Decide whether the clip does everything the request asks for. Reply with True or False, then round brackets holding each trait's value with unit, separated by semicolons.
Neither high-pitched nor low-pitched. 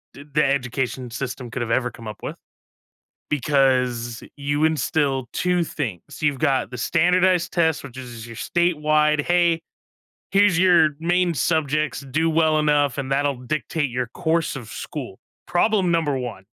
True (145 Hz)